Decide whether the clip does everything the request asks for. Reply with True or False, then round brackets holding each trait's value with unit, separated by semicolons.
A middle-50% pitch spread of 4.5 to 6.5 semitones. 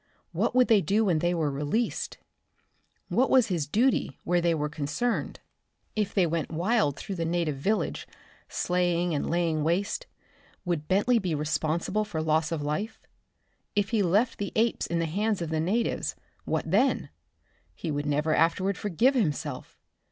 True (5.1 semitones)